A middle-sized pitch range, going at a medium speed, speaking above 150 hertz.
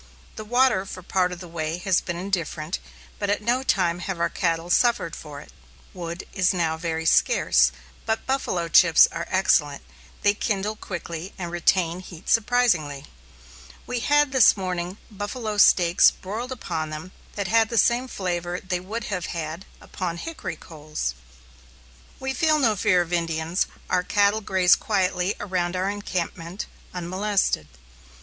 Yes: average, 3.7 semitones; average, 155 wpm; medium, 185 Hz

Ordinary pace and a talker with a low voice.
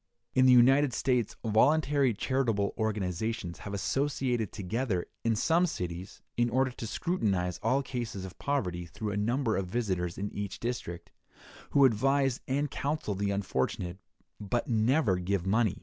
Yes: average, 150 wpm; low, 110 Hz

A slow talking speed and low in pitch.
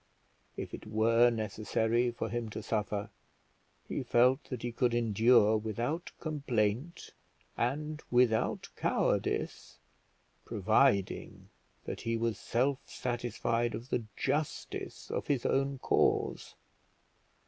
Yes: slow, 110 wpm; low, 120 Hz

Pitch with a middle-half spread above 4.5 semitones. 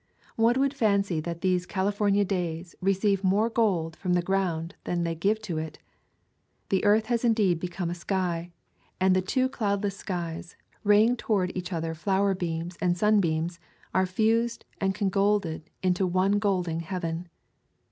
No: average, 3.0 semitones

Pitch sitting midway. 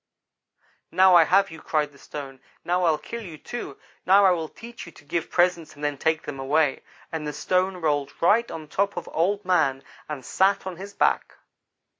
Yes: medium, 165 Hz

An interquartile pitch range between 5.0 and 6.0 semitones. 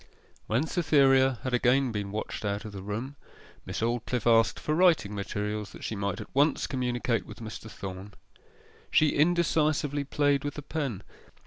Yes: wide, 5.4 semitones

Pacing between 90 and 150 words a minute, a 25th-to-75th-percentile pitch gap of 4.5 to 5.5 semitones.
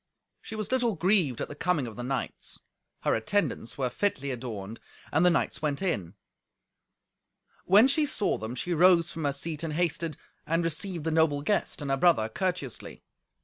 No: average, 180 wpm; average, 5.2 semitones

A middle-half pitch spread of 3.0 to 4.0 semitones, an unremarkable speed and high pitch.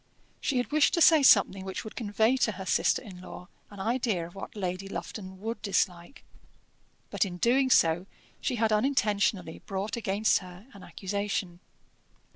Yes: average, 3.4 semitones; average, 165 wpm; high, 200 Hz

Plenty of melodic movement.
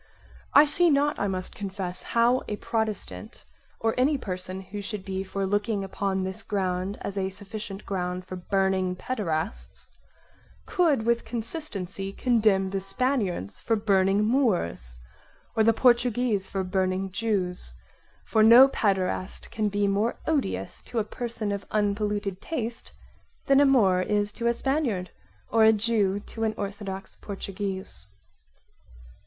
No: average, 3.2 semitones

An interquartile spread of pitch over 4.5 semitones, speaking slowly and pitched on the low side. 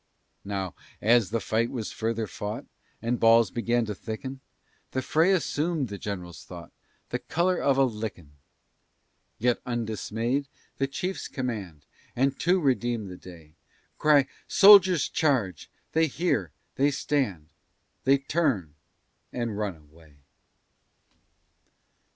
Yes: wide, 5.4 semitones; slow, 120 wpm; low, 120 Hz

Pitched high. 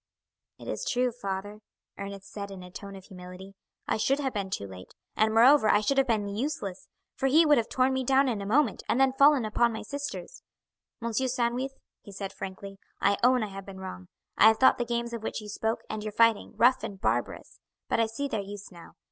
Yes: high, 220 Hz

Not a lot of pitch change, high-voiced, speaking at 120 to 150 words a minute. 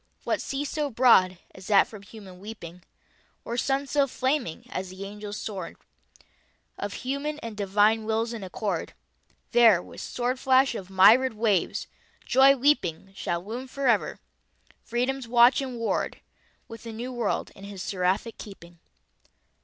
No: average, 4.6 semitones; high, 225 Hz; average, 145 wpm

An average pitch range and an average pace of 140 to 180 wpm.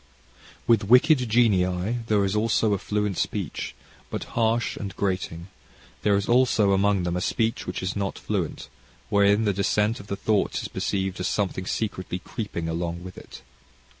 Yes: average, 3.0 semitones; average, 165 wpm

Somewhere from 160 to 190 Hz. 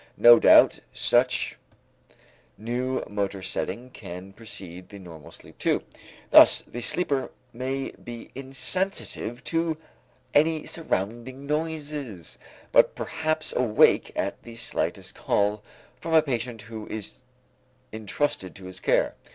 No: low, 120 Hz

